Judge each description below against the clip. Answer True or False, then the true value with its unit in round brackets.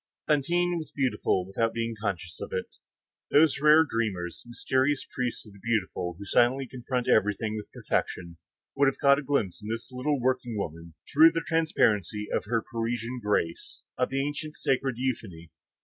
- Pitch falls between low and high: False (120 Hz)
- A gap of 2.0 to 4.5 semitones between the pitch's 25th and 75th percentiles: False (4.9 semitones)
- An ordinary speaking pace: True (170 wpm)